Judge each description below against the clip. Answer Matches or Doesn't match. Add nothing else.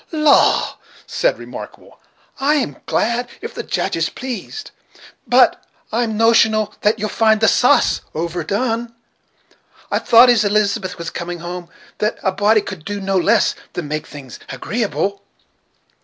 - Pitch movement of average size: Matches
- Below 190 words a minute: Matches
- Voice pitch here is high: Matches